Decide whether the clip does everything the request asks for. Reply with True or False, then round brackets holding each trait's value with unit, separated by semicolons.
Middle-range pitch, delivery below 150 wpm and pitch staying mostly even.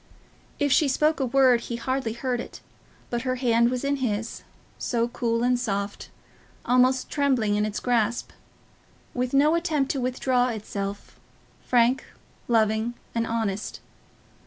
False (245 Hz; 140 wpm; 2.3 semitones)